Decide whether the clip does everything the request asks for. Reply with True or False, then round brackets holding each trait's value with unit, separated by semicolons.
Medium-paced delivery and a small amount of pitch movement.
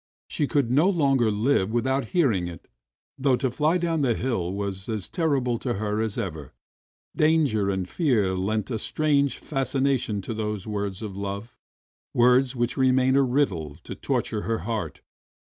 False (160 wpm; 5.1 semitones)